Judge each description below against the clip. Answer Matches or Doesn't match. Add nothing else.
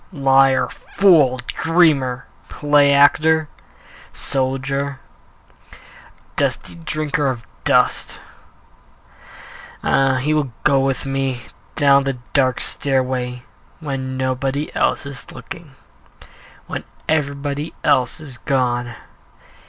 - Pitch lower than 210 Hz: Matches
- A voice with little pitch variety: Matches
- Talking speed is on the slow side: Matches